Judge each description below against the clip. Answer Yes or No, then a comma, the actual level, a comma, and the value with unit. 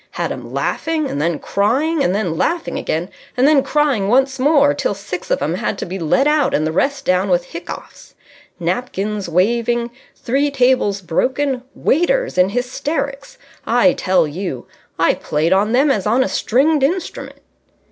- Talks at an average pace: Yes, average, 170 wpm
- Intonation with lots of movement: Yes, wide, 7.3 semitones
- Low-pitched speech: No, high, 235 Hz